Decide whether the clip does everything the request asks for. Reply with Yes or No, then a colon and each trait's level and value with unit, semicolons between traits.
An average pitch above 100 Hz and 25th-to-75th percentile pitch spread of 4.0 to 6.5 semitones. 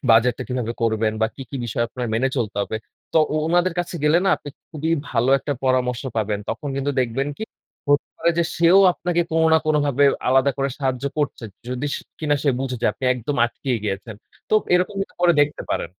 Yes: low, 135 Hz; average, 4.4 semitones